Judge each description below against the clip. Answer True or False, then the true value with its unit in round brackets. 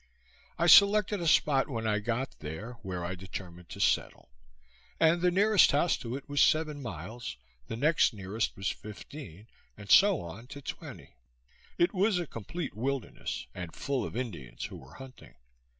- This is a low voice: True (125 Hz)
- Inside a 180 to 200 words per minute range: False (165 wpm)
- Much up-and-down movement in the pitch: True (8.6 semitones)